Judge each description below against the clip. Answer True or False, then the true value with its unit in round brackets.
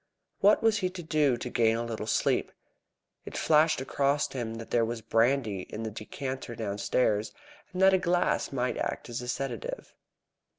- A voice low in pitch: True (125 Hz)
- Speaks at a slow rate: False (175 wpm)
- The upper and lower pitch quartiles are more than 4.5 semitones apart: True (5.2 semitones)